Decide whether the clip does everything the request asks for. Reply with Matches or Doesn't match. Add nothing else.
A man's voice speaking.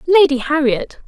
Doesn't match